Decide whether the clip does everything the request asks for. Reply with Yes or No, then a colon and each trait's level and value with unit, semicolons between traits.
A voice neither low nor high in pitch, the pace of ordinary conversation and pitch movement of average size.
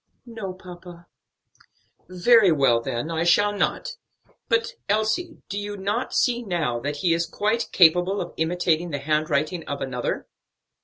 Yes: medium, 175 Hz; average, 145 wpm; average, 4.7 semitones